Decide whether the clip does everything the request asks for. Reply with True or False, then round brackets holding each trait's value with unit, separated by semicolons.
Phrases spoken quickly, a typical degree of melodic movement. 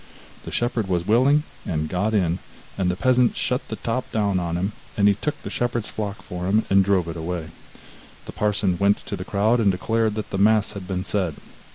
True (215 wpm; 3.3 semitones)